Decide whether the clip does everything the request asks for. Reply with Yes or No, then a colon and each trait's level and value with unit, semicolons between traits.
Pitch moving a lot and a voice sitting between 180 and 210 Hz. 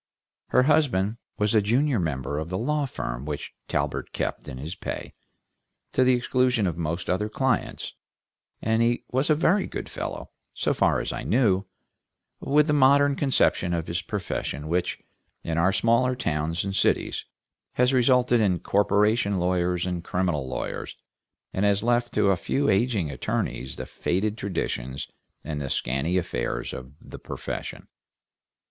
No: wide, 6.7 semitones; low, 100 Hz